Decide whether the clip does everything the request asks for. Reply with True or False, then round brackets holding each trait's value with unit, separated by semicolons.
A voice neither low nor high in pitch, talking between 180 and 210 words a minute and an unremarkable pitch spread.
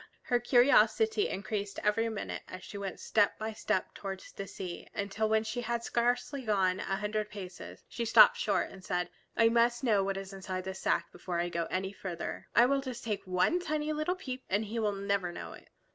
False (210 Hz; 205 wpm; 3.9 semitones)